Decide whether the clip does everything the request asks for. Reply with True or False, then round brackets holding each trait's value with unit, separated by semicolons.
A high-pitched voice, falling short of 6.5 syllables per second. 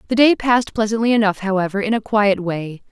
True (210 Hz; 6.0 syllables/s)